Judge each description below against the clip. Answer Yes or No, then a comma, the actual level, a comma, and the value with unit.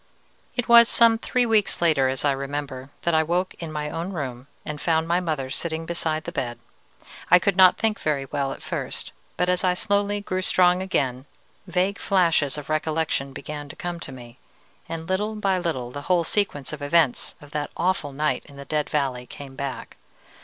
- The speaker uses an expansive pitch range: No, average, 4.6 semitones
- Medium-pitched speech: Yes, medium, 160 Hz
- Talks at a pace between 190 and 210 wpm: Yes, average, 195 wpm